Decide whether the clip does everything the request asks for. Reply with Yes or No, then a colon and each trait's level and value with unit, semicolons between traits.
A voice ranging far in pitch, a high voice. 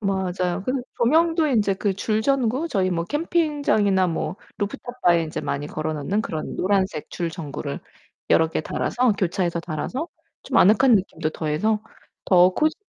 Yes: wide, 6.1 semitones; high, 195 Hz